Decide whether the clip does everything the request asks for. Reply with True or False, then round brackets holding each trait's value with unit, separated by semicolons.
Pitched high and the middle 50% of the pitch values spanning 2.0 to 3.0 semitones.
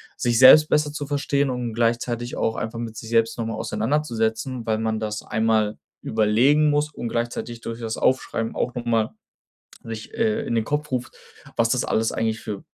False (115 Hz; 2.7 semitones)